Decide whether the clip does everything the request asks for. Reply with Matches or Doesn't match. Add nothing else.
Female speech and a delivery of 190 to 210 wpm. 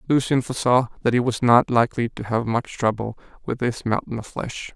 Doesn't match